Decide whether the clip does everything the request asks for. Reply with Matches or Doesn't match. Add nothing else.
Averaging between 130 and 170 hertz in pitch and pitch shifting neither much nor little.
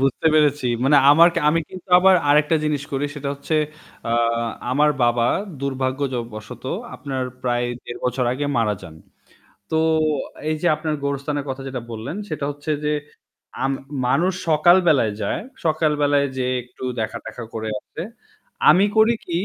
Matches